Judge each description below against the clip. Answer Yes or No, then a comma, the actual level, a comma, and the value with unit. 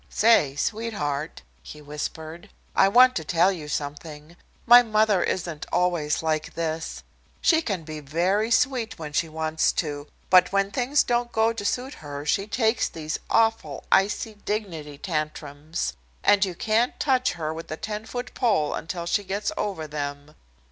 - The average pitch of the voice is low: No, medium, 175 Hz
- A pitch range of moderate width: No, wide, 6.3 semitones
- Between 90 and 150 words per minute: No, average, 160 wpm